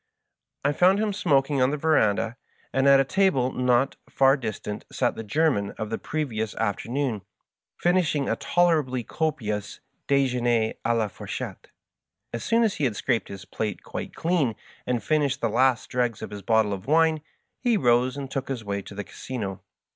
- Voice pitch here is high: No, low, 130 Hz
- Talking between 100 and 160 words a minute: No, average, 180 wpm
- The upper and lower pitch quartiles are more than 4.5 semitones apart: Yes, average, 5.1 semitones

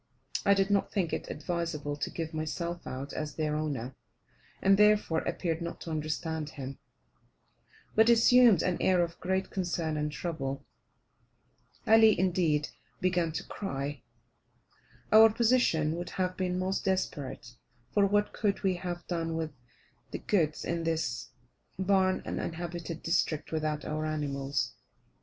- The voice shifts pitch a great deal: No, average, 3.6 semitones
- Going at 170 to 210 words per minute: No, average, 140 wpm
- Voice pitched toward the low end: No, medium, 170 Hz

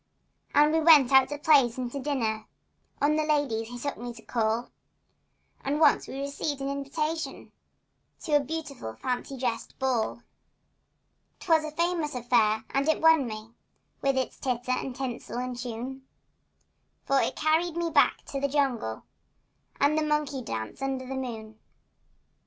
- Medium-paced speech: Yes, average, 155 wpm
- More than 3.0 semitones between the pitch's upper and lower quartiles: Yes, average, 3.6 semitones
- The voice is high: Yes, very high, 270 Hz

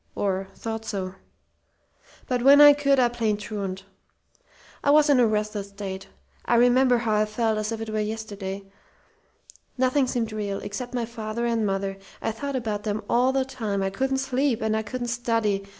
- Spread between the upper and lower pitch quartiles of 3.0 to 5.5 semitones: Yes, average, 3.3 semitones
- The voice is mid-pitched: No, high, 225 Hz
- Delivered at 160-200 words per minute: Yes, average, 180 wpm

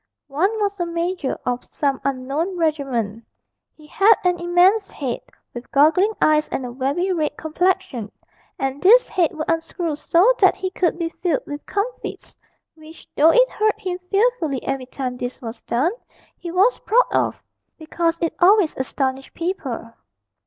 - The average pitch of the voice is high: Yes, very high, 330 Hz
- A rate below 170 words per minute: Yes, average, 160 wpm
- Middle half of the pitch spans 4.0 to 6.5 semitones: Yes, wide, 5.5 semitones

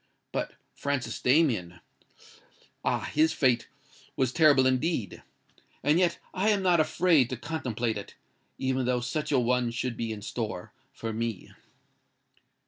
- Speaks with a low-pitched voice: Yes, low, 130 Hz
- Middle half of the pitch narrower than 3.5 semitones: No, average, 5.0 semitones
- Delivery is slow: Yes, slow, 130 wpm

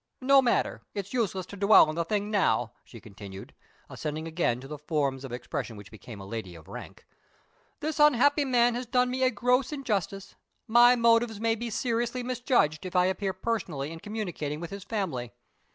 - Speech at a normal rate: Yes, average, 185 wpm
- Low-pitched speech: No, high, 200 Hz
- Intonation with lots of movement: Yes, wide, 8.4 semitones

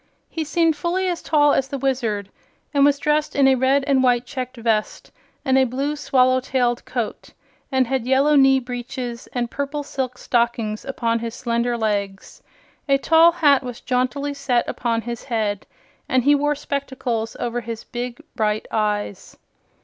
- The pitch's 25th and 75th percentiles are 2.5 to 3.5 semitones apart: Yes, average, 3.1 semitones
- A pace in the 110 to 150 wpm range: No, average, 165 wpm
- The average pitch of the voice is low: No, very high, 255 Hz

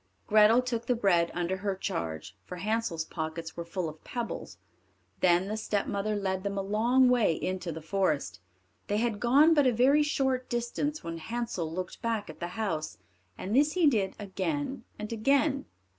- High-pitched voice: Yes, high, 210 Hz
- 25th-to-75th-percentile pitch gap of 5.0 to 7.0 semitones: Yes, wide, 5.6 semitones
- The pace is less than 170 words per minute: No, average, 175 wpm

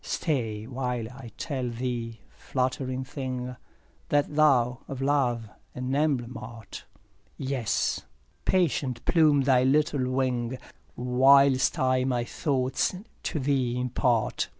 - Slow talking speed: Yes, slow, 115 wpm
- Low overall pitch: Yes, low, 130 Hz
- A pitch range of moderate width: No, narrow, 2.0 semitones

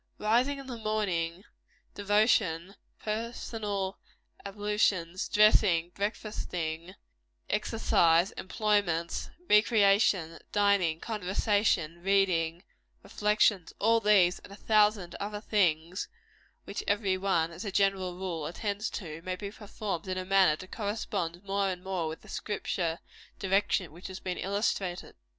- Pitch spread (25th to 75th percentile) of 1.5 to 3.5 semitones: Yes, average, 3.1 semitones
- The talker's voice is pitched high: Yes, high, 195 Hz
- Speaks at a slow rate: Yes, slow, 120 wpm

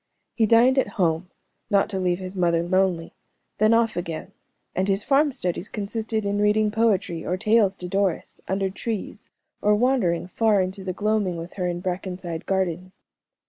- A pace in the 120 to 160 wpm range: No, average, 170 wpm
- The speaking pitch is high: Yes, high, 195 Hz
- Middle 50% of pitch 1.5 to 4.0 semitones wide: Yes, average, 3.2 semitones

